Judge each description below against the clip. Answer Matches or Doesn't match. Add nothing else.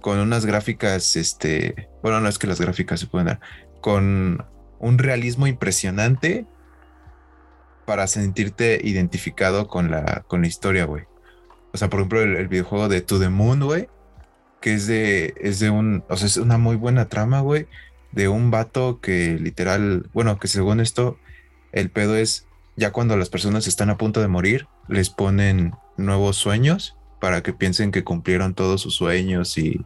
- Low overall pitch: Matches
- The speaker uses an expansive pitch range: Doesn't match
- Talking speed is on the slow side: Doesn't match